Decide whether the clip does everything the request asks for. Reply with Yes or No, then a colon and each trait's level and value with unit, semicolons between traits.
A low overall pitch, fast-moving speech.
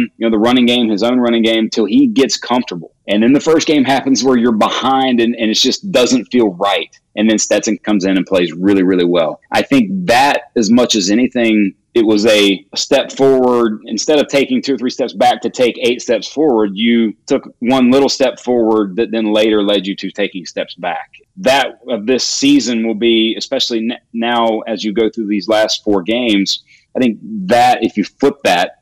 Yes: low, 115 Hz; fast, 215 wpm